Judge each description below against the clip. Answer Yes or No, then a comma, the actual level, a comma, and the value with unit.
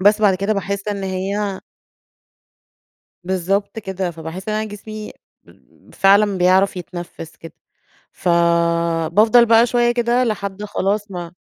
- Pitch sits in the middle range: No, high, 195 Hz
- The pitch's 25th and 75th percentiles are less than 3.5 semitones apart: Yes, average, 2.9 semitones